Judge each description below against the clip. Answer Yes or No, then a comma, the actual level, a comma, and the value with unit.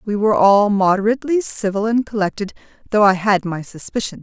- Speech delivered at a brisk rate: No, average, 170 wpm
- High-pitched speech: Yes, high, 205 Hz